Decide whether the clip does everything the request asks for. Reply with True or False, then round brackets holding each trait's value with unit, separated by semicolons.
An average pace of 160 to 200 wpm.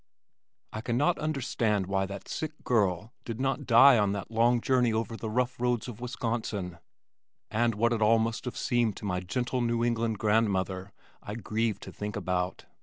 True (180 wpm)